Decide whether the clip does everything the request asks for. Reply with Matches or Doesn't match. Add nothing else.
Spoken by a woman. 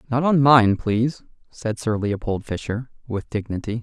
Doesn't match